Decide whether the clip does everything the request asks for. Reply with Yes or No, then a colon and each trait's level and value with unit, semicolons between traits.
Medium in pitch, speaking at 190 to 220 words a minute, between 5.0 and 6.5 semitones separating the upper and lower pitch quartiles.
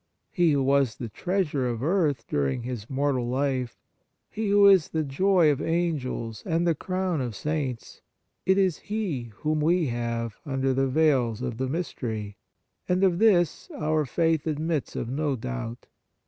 No: medium, 145 Hz; average, 160 wpm; wide, 5.6 semitones